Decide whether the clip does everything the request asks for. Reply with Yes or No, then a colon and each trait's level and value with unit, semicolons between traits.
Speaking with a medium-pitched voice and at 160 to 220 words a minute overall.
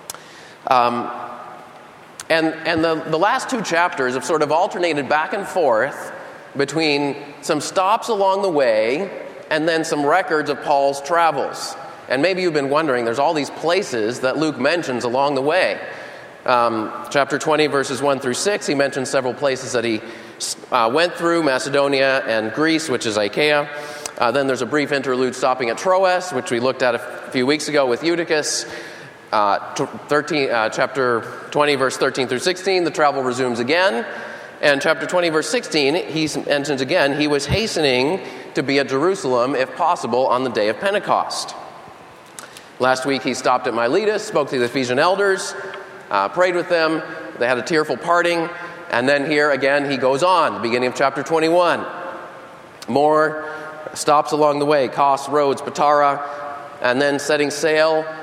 Yes: medium, 145 Hz; average, 170 wpm